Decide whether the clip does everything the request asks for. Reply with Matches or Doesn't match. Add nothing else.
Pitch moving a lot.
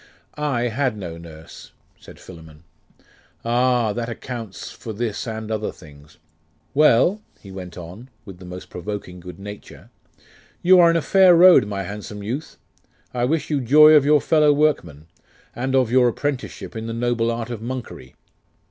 Matches